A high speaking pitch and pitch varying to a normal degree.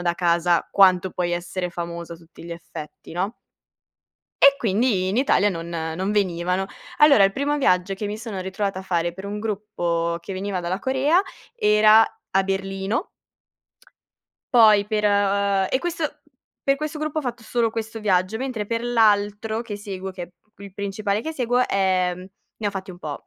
Yes: high, 200 Hz; average, 3.5 semitones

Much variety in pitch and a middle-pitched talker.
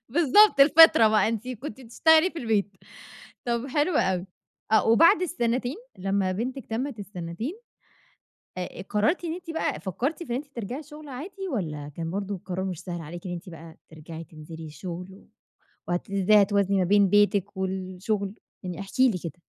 No: wide, 6.4 semitones; high, 205 Hz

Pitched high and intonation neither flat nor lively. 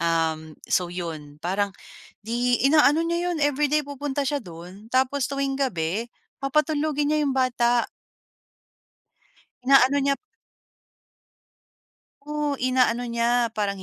No: very high, 255 Hz; wide, 5.9 semitones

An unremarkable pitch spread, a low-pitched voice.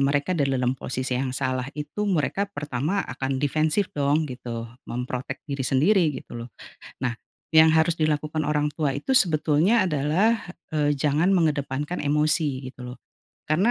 No: average, 3.2 semitones; medium, 150 Hz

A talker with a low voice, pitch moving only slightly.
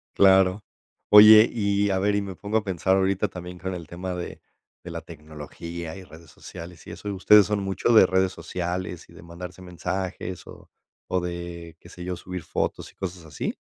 Yes: very low, 90 Hz; narrow, 2.0 semitones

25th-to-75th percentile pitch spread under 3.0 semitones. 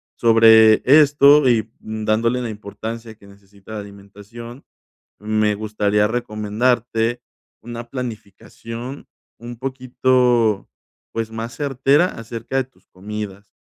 Yes: narrow, 2.6 semitones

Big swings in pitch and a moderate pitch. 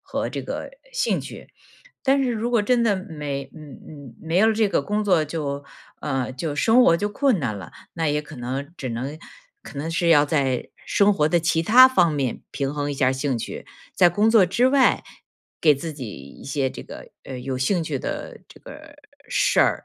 Yes: wide, 6.7 semitones; medium, 155 Hz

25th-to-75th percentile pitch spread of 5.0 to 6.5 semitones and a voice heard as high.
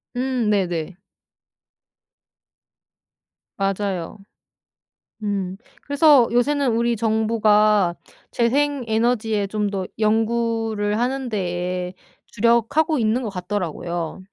No: average, 3.4 semitones; high, 215 Hz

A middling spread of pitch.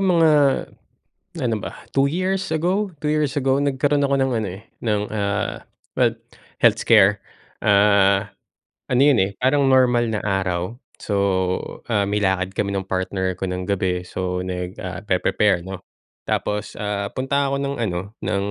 No: wide, 6.2 semitones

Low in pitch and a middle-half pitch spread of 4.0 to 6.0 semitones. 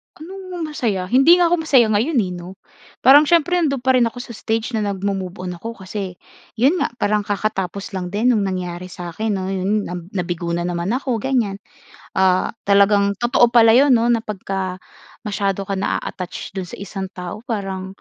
No: high, 205 Hz; average, 4.4 semitones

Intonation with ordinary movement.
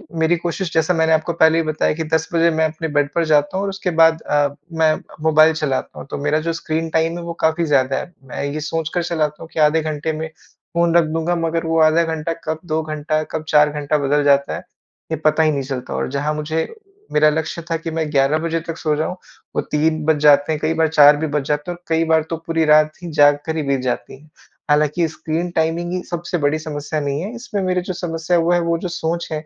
No: narrow, 1.7 semitones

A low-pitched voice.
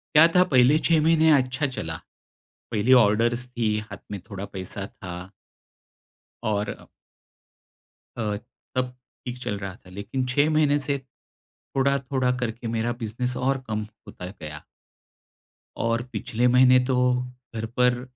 Yes: low, 125 Hz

